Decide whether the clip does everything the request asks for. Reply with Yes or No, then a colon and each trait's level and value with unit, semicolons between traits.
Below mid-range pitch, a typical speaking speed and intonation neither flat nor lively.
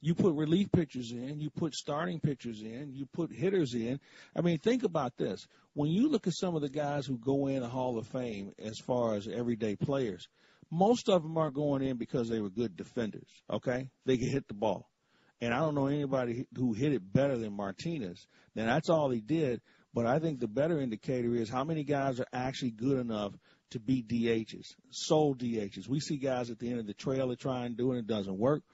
No: low, 130 Hz; fast, 220 wpm; average, 4.1 semitones